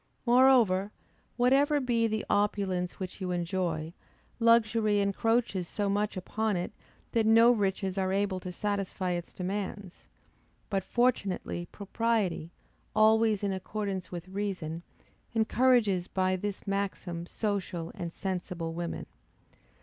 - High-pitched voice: Yes, high, 200 Hz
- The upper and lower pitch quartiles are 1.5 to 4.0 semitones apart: Yes, average, 3.1 semitones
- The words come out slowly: Yes, slow, 120 wpm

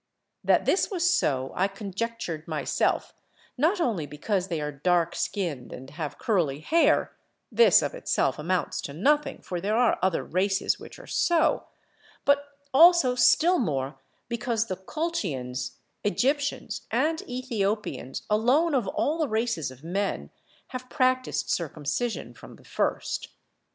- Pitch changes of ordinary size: No, wide, 8.6 semitones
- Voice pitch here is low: No, high, 205 Hz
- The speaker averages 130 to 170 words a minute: Yes, average, 140 wpm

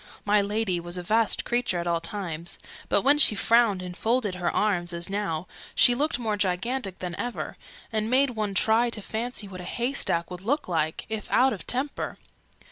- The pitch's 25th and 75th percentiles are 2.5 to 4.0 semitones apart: No, average, 5.1 semitones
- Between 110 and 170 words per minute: No, average, 195 wpm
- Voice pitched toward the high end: Yes, high, 210 Hz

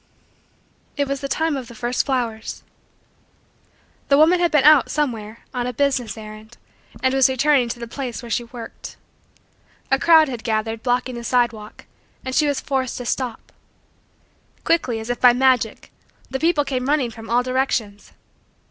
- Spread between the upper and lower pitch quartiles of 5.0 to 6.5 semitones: No, average, 3.1 semitones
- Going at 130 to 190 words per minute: Yes, average, 165 wpm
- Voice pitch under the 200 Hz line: No, very high, 250 Hz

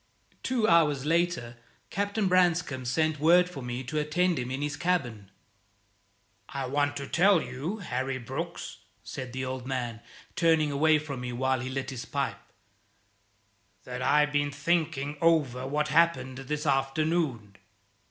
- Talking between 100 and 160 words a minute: Yes, average, 150 wpm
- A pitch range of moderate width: Yes, average, 4.1 semitones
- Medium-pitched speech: Yes, medium, 145 Hz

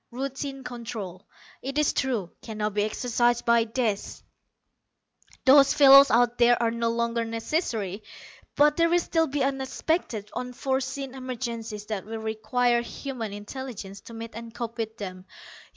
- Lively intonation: No, average, 3.3 semitones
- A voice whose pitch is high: Yes, high, 235 Hz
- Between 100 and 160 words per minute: Yes, average, 150 wpm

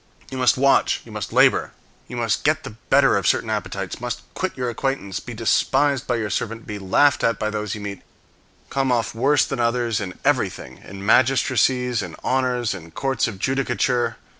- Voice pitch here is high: No, low, 120 Hz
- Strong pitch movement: No, average, 3.6 semitones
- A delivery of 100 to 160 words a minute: No, average, 190 wpm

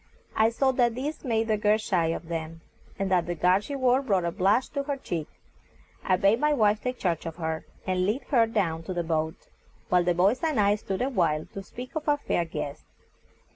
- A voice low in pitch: No, high, 200 Hz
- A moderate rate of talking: No, fast, 225 wpm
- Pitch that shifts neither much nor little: No, wide, 6.4 semitones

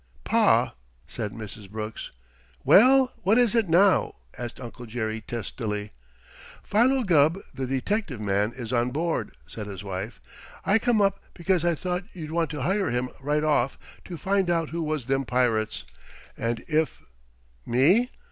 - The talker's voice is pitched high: No, medium, 145 Hz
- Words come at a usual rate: Yes, average, 160 wpm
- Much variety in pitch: Yes, wide, 8.5 semitones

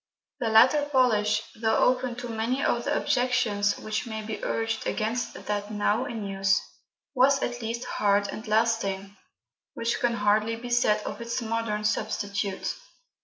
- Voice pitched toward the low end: No, high, 225 Hz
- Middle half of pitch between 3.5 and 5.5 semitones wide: No, narrow, 2.5 semitones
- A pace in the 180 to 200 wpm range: No, average, 155 wpm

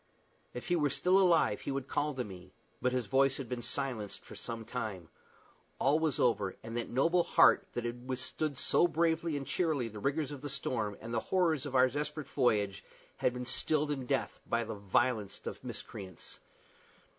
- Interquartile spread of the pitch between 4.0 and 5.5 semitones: Yes, average, 4.5 semitones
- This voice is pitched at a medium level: No, low, 130 Hz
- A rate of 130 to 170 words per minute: No, average, 190 wpm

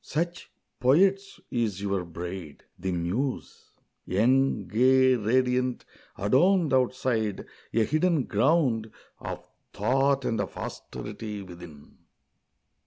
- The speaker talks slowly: Yes, slow, 100 wpm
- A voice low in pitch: Yes, low, 120 Hz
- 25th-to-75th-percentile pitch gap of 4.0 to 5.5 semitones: Yes, average, 5.2 semitones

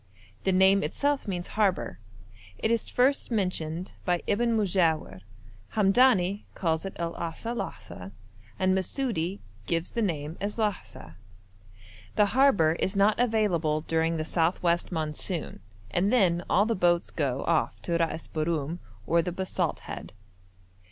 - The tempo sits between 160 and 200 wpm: No, average, 140 wpm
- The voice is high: No, medium, 180 Hz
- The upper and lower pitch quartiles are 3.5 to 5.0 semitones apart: Yes, average, 4.2 semitones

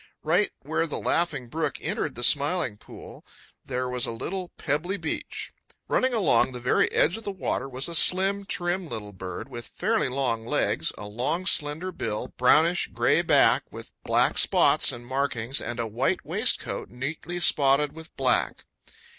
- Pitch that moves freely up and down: Yes, wide, 6.3 semitones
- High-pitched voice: No, medium, 140 Hz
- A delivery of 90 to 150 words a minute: No, average, 165 wpm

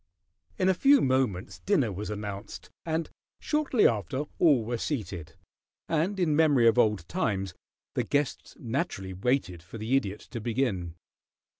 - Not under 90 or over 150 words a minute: Yes, average, 145 wpm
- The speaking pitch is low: Yes, low, 120 Hz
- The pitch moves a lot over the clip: Yes, wide, 7.2 semitones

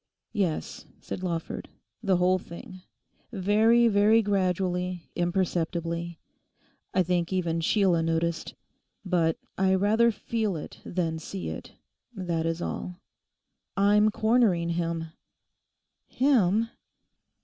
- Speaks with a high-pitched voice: No, medium, 180 Hz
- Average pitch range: Yes, average, 3.3 semitones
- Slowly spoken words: Yes, slow, 100 wpm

